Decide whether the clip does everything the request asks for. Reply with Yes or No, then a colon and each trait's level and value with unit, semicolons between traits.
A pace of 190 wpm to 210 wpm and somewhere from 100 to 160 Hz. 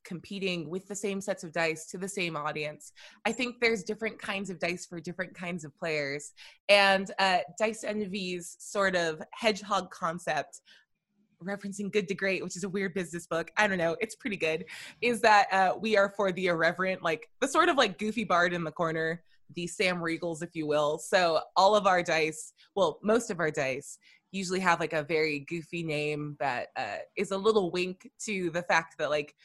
No: average, 200 wpm; medium, 185 Hz